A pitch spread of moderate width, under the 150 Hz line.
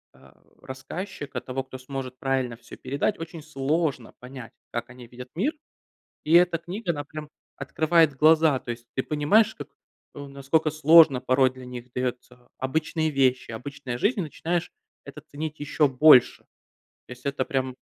Yes: average, 3.7 semitones; medium, 140 Hz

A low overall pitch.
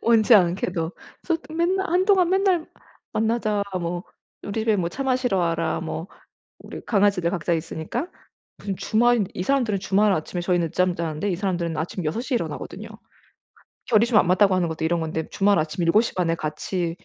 No: high, 190 Hz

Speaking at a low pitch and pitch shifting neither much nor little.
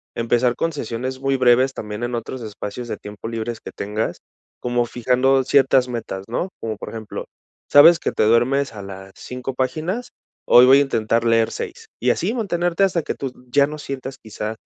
Yes: low, 125 Hz; average, 3.3 semitones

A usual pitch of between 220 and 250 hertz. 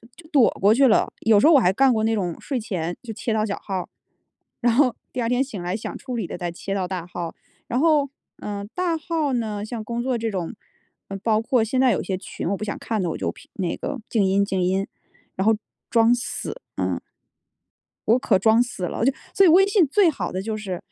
Yes: high, 225 Hz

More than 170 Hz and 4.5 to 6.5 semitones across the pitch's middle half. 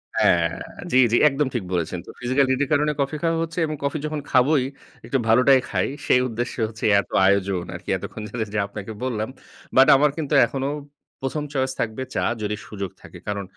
No: low, 130 Hz; average, 4.8 semitones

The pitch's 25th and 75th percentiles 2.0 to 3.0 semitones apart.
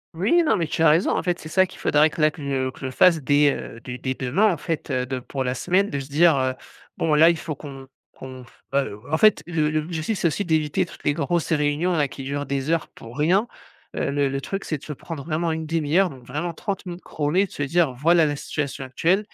No: average, 3.7 semitones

